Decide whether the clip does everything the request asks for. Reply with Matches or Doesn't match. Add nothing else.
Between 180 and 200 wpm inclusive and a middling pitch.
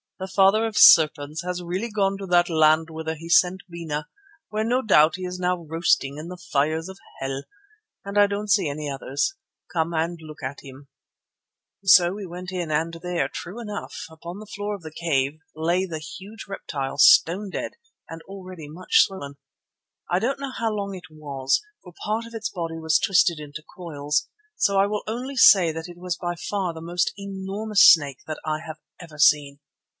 Matches